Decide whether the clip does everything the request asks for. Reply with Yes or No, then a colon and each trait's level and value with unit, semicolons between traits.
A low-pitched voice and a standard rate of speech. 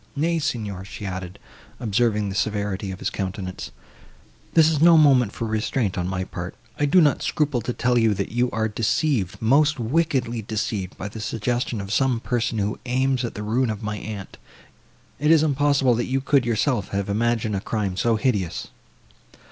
Yes: low, 115 Hz; average, 180 wpm